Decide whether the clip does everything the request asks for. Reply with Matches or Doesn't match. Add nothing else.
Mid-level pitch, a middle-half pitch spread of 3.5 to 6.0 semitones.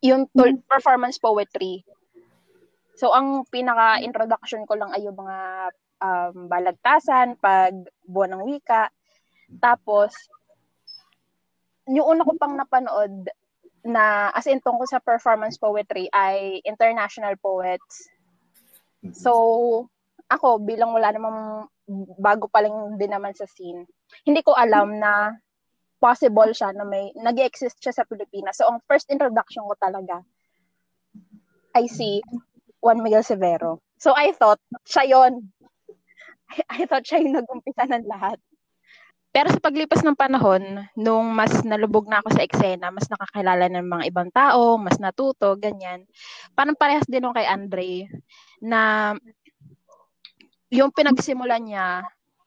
Doesn't match